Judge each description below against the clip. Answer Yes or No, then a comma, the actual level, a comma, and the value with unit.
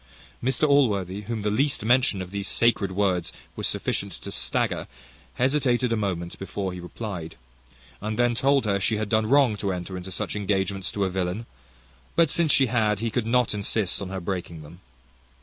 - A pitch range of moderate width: Yes, average, 4.1 semitones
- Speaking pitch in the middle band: No, low, 105 Hz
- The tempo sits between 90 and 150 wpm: No, average, 185 wpm